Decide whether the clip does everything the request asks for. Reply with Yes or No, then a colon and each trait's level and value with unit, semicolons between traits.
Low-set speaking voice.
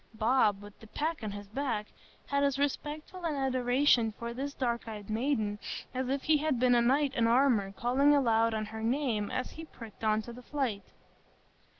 No: high, 245 Hz